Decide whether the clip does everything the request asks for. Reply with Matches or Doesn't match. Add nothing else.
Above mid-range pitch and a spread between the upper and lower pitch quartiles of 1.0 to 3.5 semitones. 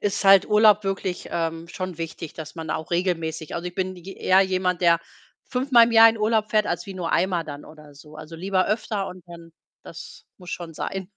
Doesn't match